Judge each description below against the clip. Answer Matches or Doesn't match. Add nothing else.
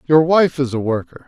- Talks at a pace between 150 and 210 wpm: Doesn't match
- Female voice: Doesn't match